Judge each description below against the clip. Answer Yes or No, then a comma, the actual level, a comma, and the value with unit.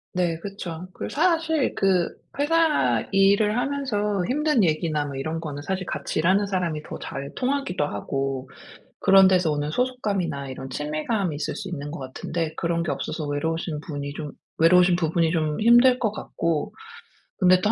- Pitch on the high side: No, medium, 175 Hz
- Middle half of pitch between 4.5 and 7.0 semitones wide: Yes, wide, 5.4 semitones